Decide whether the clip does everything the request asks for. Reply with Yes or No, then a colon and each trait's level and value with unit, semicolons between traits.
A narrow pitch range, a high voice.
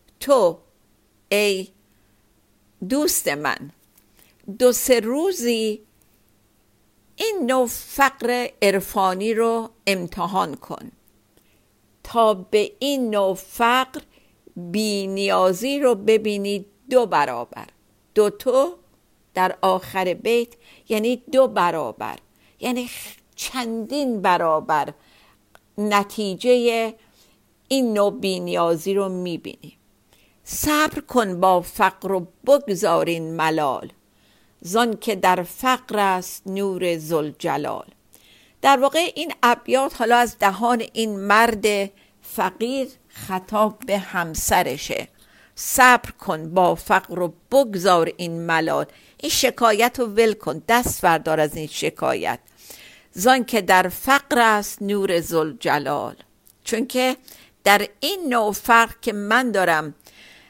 No: average, 5.1 semitones; high, 205 Hz